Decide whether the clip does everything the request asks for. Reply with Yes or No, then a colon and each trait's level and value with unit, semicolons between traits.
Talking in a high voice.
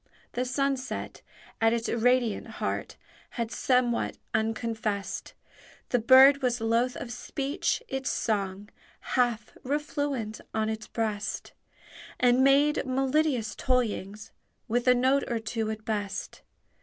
Yes: high, 240 Hz